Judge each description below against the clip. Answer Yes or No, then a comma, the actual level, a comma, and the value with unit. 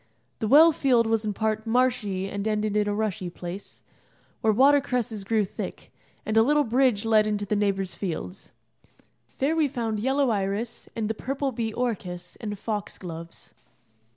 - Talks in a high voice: Yes, high, 220 Hz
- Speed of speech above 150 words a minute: Yes, average, 170 wpm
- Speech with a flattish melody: No, average, 3.5 semitones